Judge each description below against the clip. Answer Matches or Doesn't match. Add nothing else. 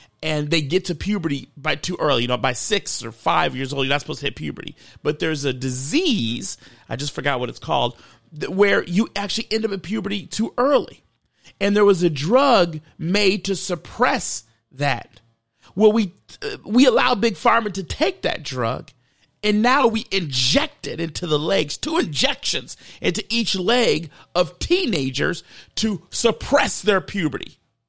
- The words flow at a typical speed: Matches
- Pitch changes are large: Matches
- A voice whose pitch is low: Doesn't match